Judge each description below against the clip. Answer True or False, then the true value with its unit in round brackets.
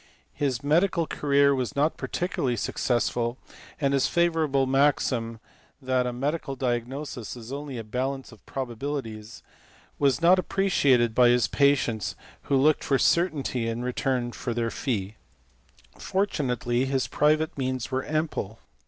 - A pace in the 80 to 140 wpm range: True (135 wpm)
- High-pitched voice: False (135 Hz)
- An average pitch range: True (3.3 semitones)